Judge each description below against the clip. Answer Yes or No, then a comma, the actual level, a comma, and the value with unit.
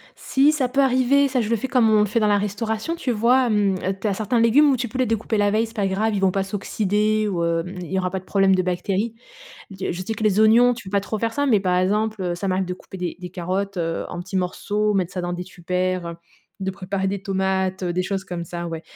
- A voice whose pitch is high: Yes, high, 200 Hz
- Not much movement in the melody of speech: No, average, 3.2 semitones